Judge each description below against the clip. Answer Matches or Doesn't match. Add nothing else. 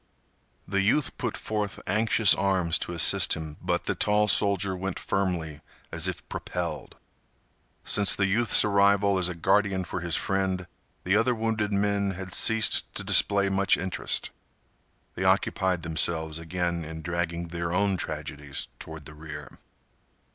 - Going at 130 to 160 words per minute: Matches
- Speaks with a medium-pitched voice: Doesn't match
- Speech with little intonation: Doesn't match